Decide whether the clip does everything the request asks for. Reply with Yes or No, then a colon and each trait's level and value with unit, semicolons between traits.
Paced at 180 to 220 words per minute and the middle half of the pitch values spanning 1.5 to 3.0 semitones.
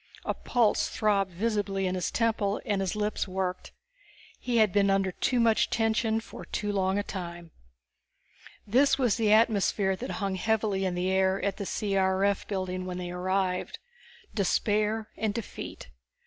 No: average, 160 wpm; narrow, 2.5 semitones